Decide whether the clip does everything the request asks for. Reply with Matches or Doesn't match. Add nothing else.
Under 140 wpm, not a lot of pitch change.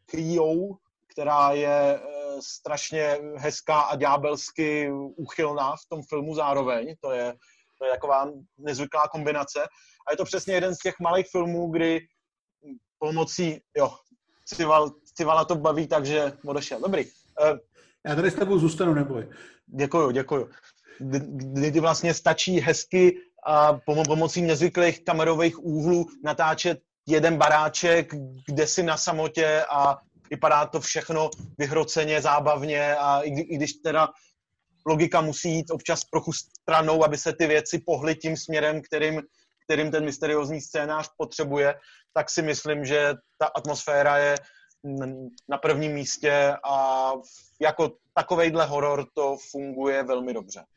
Matches